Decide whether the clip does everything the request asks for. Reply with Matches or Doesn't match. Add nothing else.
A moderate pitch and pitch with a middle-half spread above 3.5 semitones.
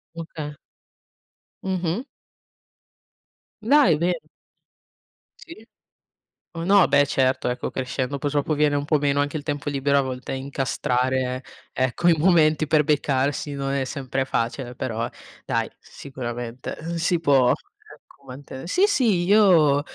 Matches